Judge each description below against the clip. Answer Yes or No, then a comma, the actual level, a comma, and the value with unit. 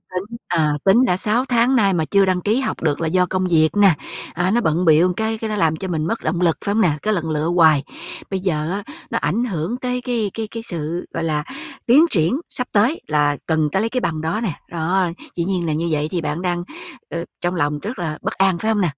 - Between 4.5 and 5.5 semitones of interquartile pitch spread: Yes, average, 5.1 semitones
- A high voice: No, medium, 180 Hz